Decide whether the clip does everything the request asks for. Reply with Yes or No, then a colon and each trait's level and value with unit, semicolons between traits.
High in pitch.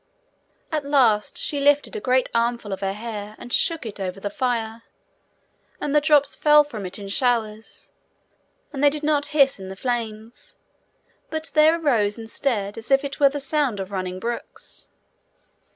Yes: high, 240 Hz